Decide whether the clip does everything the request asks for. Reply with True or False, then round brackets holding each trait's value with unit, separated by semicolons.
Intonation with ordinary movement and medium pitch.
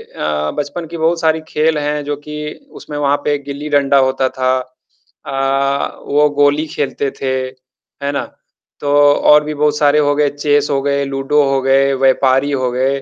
False (1.5 semitones; 145 Hz)